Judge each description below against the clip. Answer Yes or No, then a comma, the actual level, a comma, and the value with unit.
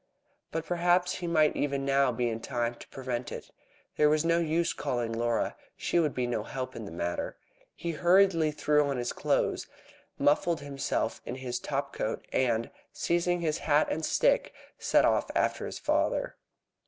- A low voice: No, medium, 145 Hz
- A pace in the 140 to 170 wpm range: No, average, 180 wpm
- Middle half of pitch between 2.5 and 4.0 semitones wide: No, average, 5.3 semitones